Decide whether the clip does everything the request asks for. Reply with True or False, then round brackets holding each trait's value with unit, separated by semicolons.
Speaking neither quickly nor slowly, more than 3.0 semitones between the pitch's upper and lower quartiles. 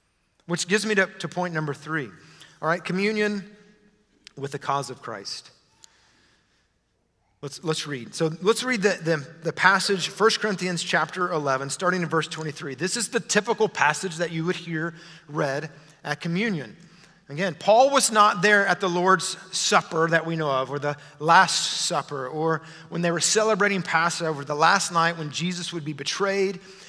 True (170 wpm; 3.7 semitones)